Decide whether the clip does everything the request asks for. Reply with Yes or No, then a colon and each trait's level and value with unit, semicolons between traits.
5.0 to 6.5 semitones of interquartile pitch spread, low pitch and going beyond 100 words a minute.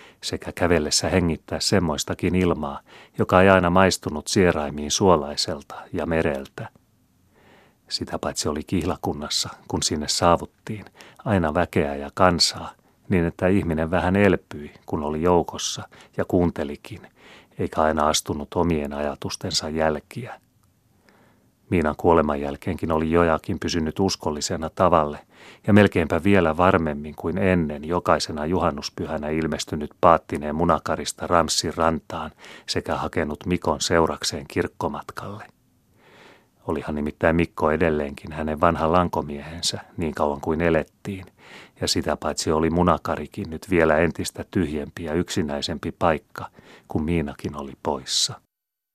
No: average, 3.0 semitones; very low, 80 Hz; average, 115 wpm